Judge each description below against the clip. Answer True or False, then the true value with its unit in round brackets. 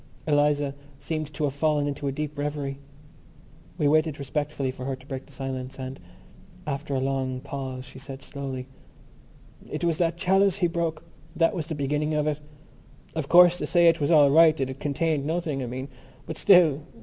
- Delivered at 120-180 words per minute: False (190 wpm)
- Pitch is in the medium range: True (145 Hz)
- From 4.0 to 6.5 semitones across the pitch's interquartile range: False (2.7 semitones)